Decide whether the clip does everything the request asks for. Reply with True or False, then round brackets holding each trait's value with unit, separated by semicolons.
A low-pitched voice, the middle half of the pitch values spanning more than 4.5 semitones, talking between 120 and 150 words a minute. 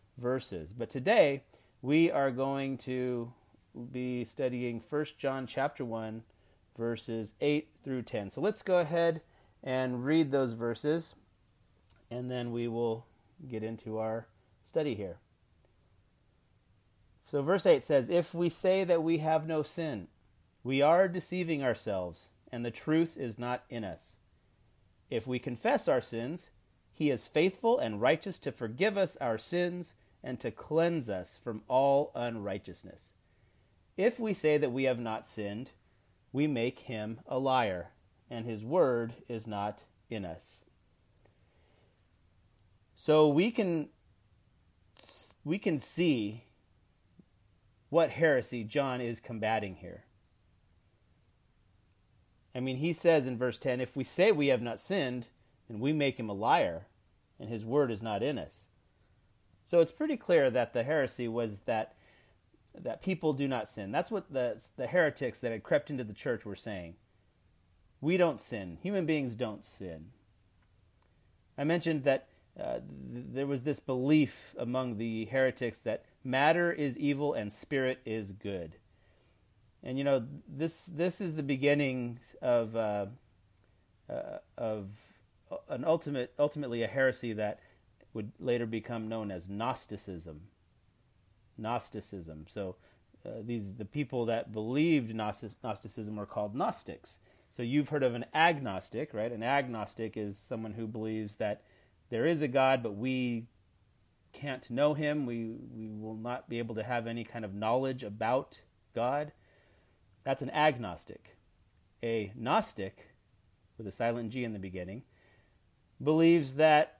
True (115 Hz; 5.2 semitones; 145 wpm)